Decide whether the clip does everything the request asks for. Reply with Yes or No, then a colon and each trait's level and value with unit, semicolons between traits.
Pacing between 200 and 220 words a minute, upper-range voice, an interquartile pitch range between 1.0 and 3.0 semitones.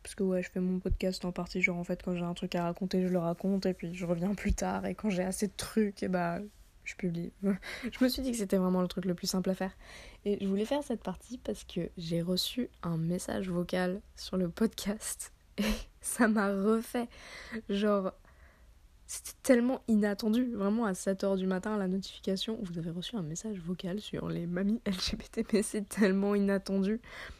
Yes: average, 210 wpm; high, 195 Hz; narrow, 2.6 semitones